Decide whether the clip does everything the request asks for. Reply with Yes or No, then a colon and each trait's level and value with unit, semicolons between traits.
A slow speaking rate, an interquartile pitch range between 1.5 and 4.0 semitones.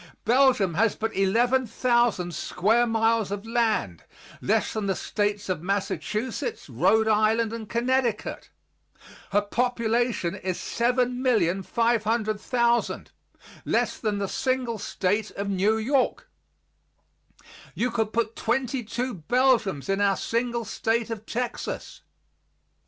Yes: slow, 110 wpm; average, 2.9 semitones